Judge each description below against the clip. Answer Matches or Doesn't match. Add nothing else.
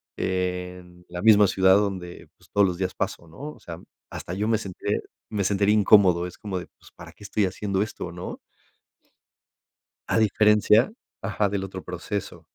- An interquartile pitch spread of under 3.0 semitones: Matches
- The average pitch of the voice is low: Matches